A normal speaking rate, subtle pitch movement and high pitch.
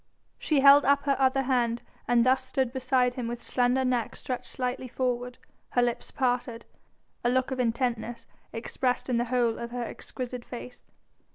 Yes: average, 170 wpm; narrow, 1.3 semitones; very high, 250 Hz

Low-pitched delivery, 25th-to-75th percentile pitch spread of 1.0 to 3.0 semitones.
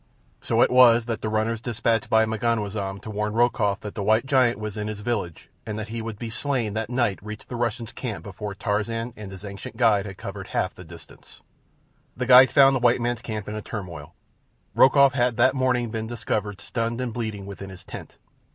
Yes: low, 110 Hz; narrow, 2.5 semitones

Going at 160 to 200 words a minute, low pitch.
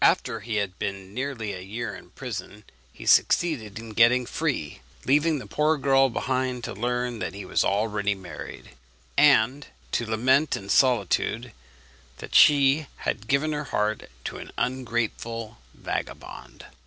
No: average, 145 wpm; low, 120 Hz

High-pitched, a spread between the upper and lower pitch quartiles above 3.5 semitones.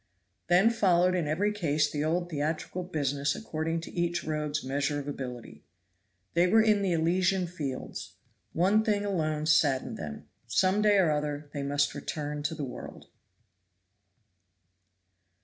No: medium, 160 Hz; average, 3.9 semitones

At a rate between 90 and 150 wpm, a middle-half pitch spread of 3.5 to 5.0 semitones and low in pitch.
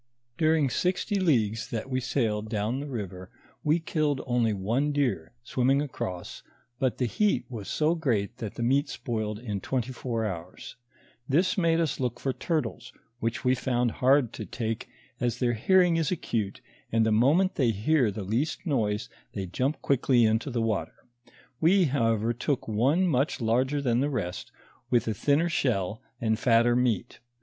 No: average, 170 wpm; average, 4.6 semitones; low, 125 Hz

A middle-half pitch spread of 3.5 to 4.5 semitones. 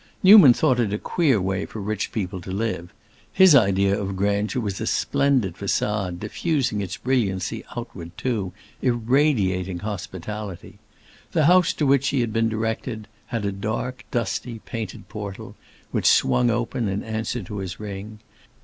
Yes: average, 4.1 semitones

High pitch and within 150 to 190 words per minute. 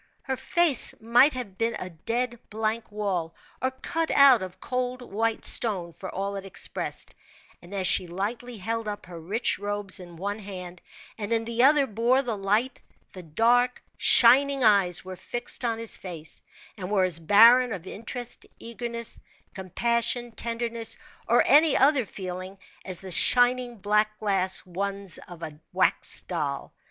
Yes: high, 215 Hz; average, 160 wpm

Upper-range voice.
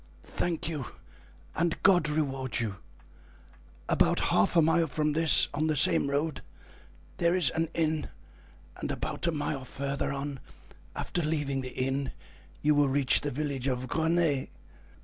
No: medium, 145 Hz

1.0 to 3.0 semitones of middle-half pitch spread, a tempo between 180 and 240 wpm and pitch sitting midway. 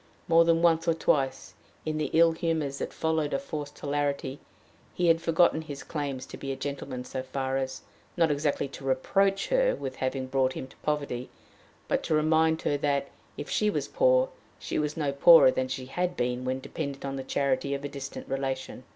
No: average, 3.4 semitones; average, 200 wpm; medium, 145 Hz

